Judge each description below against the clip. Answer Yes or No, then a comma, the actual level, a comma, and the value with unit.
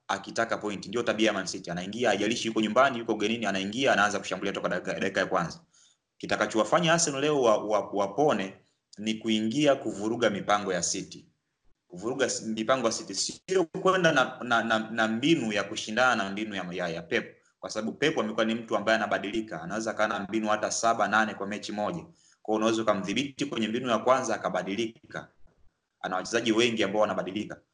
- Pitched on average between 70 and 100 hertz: No, low, 110 Hz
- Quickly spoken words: Yes, fast, 155 wpm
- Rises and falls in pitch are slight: Yes, narrow, 1.9 semitones